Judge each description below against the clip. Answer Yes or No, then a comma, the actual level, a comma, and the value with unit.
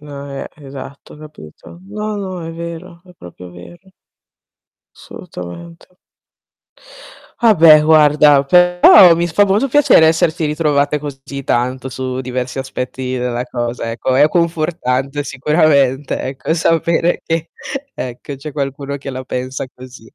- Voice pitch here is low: No, medium, 145 Hz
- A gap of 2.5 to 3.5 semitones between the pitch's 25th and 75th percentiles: No, average, 4.4 semitones